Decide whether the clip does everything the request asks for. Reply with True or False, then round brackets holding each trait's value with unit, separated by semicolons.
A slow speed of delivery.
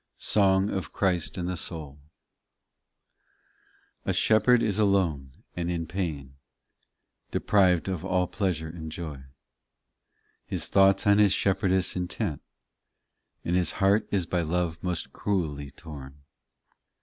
True (125 wpm)